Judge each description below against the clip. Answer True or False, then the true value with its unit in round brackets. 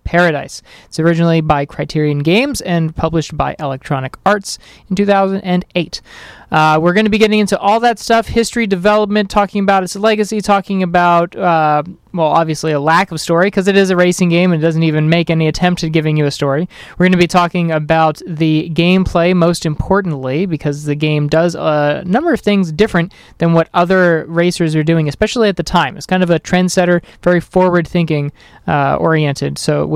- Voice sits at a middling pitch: True (170 Hz)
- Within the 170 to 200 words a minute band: True (195 wpm)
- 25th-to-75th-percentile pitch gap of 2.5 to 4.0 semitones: True (3.3 semitones)